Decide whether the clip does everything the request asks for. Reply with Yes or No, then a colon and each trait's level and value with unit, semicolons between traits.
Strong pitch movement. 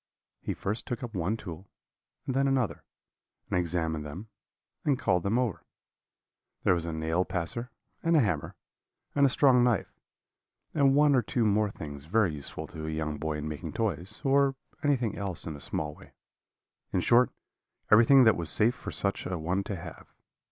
Yes: wide, 7.2 semitones